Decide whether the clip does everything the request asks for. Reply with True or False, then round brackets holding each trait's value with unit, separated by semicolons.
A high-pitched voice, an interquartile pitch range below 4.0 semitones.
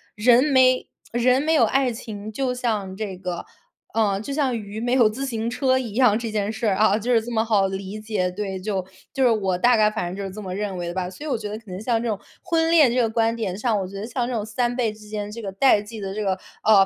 True (220 Hz; 3.3 semitones)